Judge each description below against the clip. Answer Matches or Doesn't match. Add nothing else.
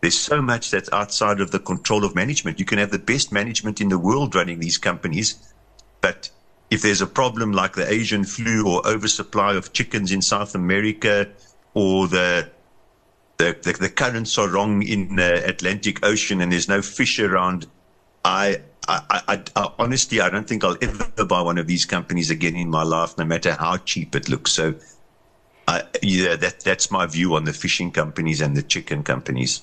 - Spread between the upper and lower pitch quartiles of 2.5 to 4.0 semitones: Matches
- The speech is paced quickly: Doesn't match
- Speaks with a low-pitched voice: Matches